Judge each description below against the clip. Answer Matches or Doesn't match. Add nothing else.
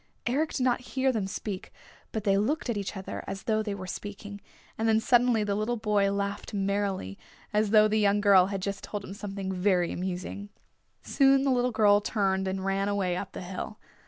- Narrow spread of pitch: Matches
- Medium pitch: Doesn't match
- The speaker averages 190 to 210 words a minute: Matches